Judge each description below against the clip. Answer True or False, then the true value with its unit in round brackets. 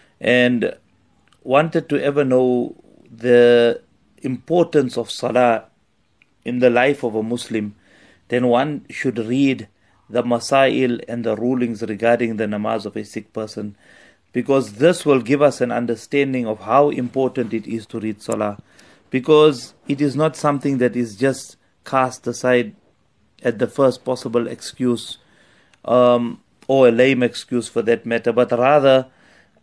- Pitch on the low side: True (125 Hz)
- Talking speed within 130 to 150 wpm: True (145 wpm)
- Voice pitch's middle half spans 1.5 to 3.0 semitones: True (2.7 semitones)